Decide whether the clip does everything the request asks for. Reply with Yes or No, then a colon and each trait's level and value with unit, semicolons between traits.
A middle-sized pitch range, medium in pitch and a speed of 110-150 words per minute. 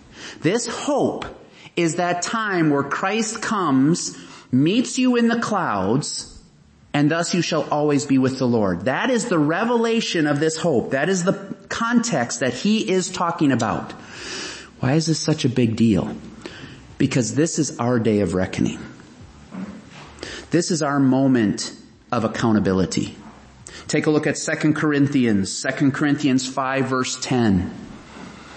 No: wide, 5.8 semitones; medium, 150 Hz; average, 145 wpm